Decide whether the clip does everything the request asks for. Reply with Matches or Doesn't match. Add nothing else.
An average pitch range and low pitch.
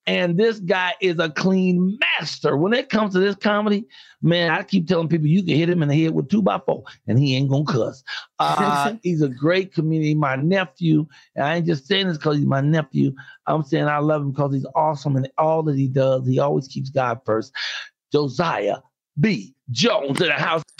Doesn't match